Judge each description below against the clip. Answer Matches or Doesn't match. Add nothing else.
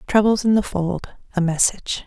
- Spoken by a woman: Matches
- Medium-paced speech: Matches